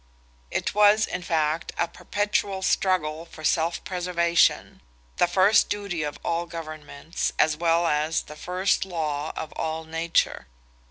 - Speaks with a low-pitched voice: No, medium, 170 Hz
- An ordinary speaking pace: No, slow, 130 wpm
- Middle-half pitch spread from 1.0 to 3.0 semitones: Yes, average, 2.7 semitones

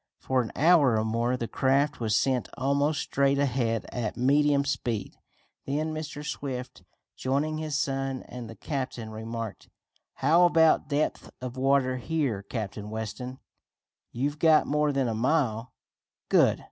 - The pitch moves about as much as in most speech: Yes, average, 3.8 semitones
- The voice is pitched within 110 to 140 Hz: Yes, low, 135 Hz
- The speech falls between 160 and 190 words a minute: No, average, 145 wpm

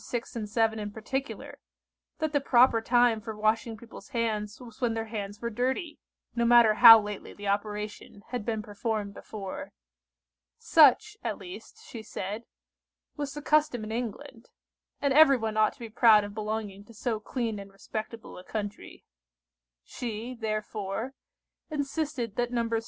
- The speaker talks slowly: No, average, 155 wpm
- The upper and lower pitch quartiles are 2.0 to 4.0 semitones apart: Yes, average, 2.9 semitones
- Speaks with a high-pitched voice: Yes, high, 225 Hz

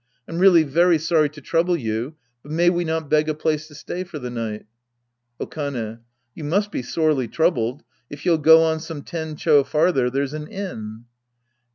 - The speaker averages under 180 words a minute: No, average, 185 wpm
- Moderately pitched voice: Yes, medium, 155 Hz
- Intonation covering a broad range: No, average, 3.2 semitones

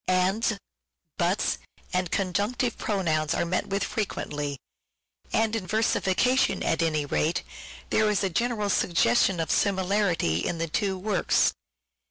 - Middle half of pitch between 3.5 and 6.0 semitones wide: Yes, average, 4.2 semitones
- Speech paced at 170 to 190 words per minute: No, average, 140 wpm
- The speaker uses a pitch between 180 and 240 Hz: Yes, high, 190 Hz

